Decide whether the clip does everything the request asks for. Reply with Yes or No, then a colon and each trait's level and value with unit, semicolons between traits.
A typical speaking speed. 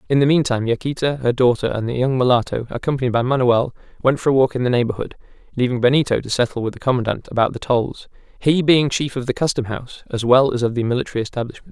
No: fast, 220 wpm